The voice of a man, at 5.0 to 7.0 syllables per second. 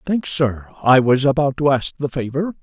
No: male; 4.7 syllables/s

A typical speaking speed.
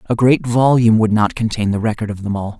No: fast, 255 wpm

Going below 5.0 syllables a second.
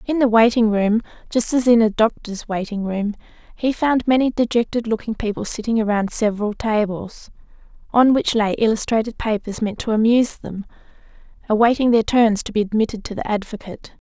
No: 5.5 syllables/s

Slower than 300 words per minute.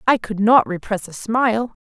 Yes: average, 200 wpm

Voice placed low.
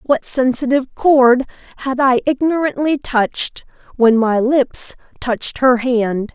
No: very high, 255 Hz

